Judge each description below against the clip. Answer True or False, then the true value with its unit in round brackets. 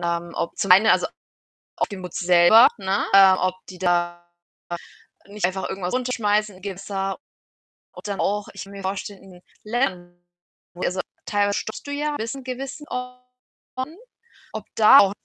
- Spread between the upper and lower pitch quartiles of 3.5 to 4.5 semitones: True (3.9 semitones)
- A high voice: True (195 Hz)